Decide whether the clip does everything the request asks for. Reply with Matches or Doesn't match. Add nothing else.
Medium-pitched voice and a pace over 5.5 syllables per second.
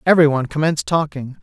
Matches